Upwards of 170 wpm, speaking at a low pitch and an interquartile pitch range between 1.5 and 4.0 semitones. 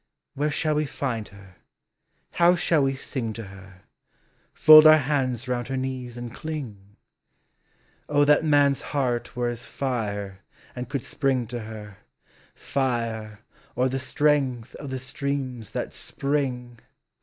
No: average, 140 wpm; low, 130 Hz; average, 3.6 semitones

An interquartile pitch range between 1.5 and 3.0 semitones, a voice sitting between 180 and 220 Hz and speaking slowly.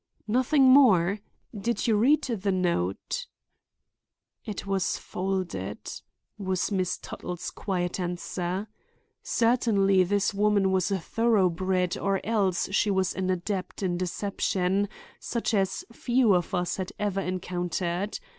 Yes: narrow, 2.4 semitones; high, 190 Hz; slow, 120 wpm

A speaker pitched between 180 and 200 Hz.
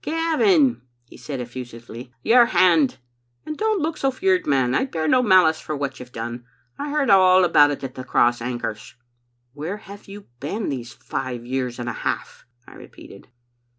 No: medium, 145 Hz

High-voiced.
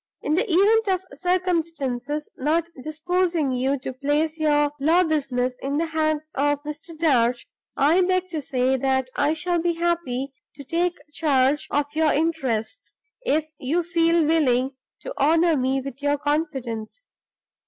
Yes: very high, 305 Hz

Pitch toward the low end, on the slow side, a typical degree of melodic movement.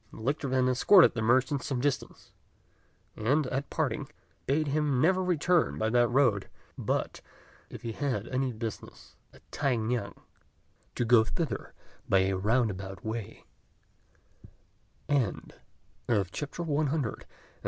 Yes: low, 125 Hz; slow, 115 wpm; average, 4.4 semitones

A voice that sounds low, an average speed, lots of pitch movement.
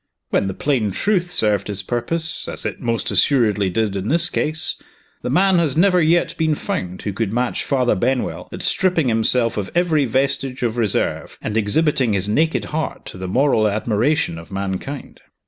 Yes: low, 125 Hz; average, 180 wpm; wide, 7.1 semitones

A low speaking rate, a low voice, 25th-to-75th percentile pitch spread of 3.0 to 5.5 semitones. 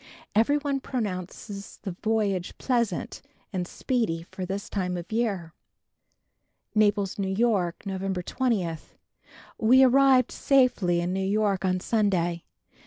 No: slow, 120 wpm; high, 200 Hz; average, 4.3 semitones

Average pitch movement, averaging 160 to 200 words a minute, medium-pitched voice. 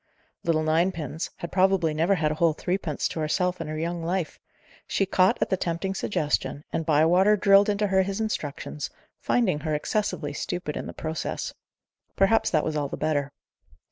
Yes: average, 3.8 semitones; average, 175 wpm; medium, 170 Hz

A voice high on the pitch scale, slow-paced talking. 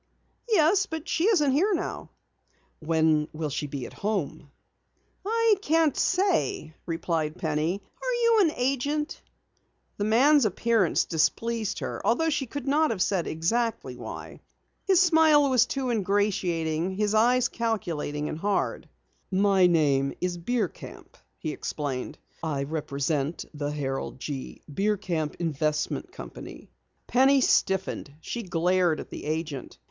Yes: high, 195 Hz; slow, 130 wpm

